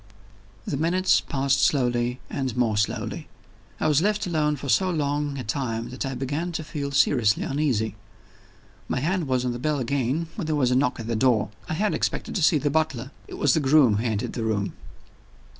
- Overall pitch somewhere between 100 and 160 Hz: Yes, low, 135 Hz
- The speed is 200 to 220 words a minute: Yes, fast, 205 wpm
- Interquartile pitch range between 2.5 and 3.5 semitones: No, average, 4.0 semitones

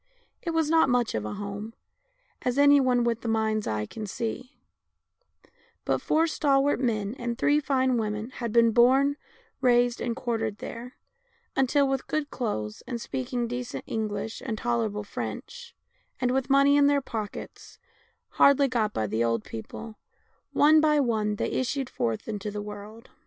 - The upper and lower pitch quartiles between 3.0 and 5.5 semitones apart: Yes, average, 4.0 semitones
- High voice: Yes, high, 240 Hz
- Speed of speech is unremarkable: Yes, average, 160 wpm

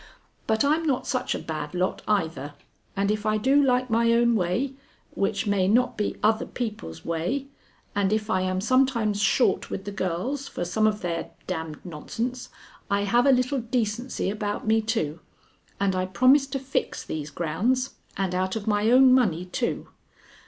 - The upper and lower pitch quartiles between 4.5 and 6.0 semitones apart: Yes, average, 5.2 semitones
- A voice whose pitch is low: No, high, 215 Hz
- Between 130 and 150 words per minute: No, average, 180 wpm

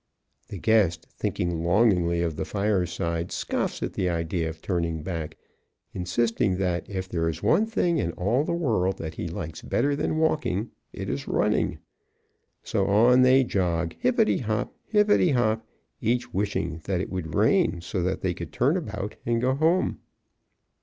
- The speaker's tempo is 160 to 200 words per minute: Yes, average, 165 wpm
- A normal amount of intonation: No, wide, 5.9 semitones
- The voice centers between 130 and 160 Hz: No, very low, 95 Hz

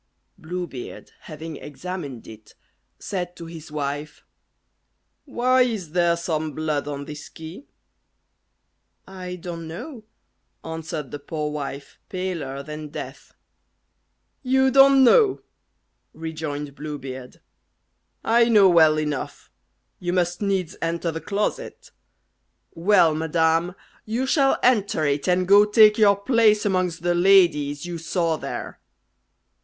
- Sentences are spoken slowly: Yes, slow, 120 wpm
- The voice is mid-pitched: Yes, medium, 170 Hz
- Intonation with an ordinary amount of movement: Yes, average, 4.6 semitones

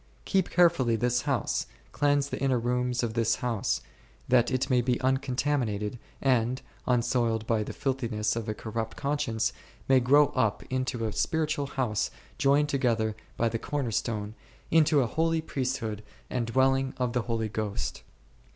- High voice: No, low, 125 Hz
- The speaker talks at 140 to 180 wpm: Yes, average, 160 wpm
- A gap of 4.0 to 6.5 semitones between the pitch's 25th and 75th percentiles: No, average, 3.3 semitones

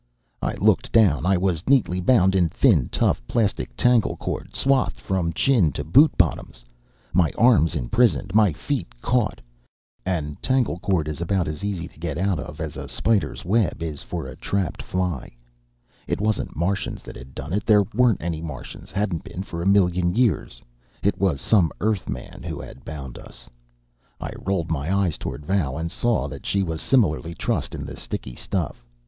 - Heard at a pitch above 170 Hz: No, very low, 90 Hz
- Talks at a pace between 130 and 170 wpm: No, average, 180 wpm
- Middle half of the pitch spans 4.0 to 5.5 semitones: Yes, average, 4.7 semitones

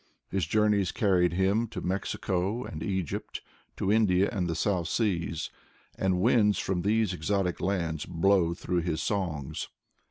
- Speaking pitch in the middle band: No, very low, 95 Hz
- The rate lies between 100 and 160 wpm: Yes, average, 140 wpm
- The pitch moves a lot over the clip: No, average, 2.9 semitones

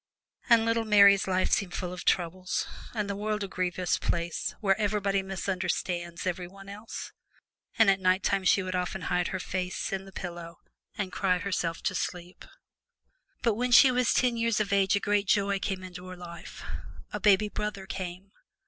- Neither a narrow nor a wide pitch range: No, narrow, 2.1 semitones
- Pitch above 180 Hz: Yes, high, 190 Hz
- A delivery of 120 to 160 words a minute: No, average, 175 wpm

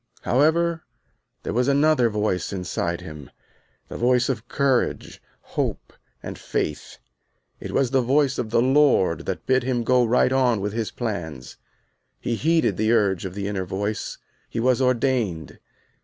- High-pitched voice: No, low, 120 Hz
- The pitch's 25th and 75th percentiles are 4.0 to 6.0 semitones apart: Yes, average, 4.7 semitones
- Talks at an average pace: Yes, average, 155 wpm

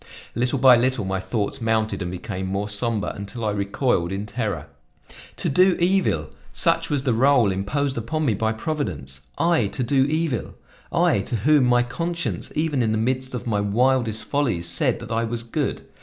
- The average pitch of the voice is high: No, low, 115 Hz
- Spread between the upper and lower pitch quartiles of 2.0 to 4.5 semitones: No, average, 5.0 semitones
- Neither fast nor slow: Yes, average, 185 wpm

